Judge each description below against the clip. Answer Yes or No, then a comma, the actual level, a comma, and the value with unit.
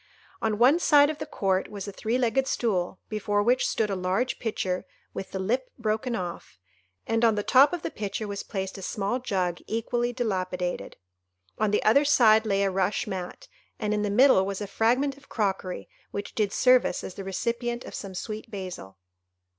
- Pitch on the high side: Yes, high, 210 Hz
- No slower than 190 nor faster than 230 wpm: Yes, average, 195 wpm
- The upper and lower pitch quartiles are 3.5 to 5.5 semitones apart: Yes, average, 3.8 semitones